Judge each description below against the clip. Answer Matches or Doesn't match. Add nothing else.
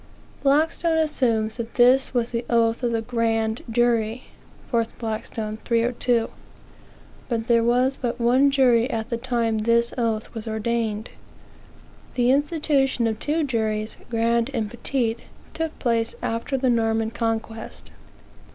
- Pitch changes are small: Matches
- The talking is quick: Doesn't match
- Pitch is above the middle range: Matches